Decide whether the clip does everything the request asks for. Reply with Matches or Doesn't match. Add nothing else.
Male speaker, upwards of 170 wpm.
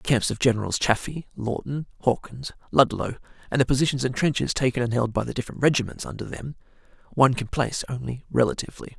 Matches